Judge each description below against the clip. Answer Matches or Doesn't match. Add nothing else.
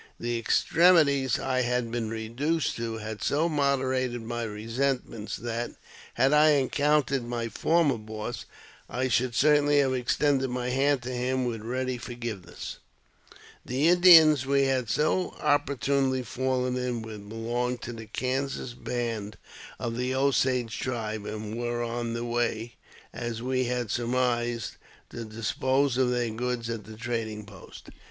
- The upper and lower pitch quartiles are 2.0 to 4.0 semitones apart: Matches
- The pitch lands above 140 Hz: Doesn't match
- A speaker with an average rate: Matches